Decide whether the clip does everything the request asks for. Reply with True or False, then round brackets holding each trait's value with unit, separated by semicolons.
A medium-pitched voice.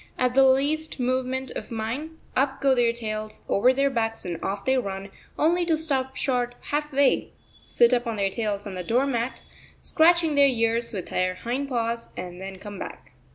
False (245 Hz)